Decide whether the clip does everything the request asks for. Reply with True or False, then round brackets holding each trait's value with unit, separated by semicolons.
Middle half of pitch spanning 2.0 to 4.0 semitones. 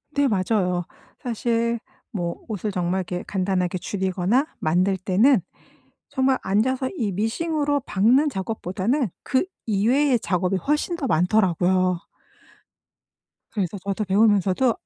False (5.6 semitones)